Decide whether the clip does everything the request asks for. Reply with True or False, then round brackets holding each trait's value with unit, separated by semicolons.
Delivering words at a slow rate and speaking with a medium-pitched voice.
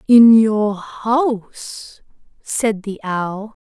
False (100 wpm; 215 Hz)